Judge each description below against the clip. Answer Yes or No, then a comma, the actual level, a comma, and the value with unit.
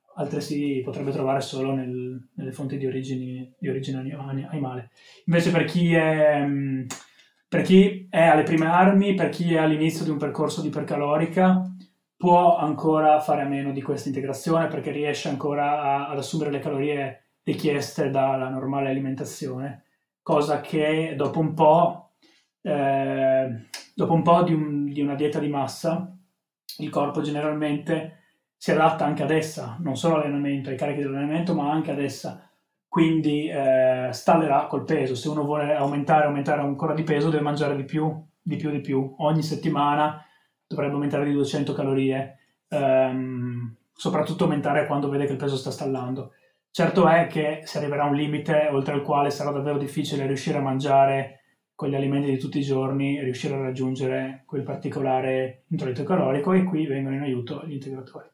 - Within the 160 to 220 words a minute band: Yes, fast, 170 wpm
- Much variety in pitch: No, narrow, 2.4 semitones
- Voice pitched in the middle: Yes, medium, 145 Hz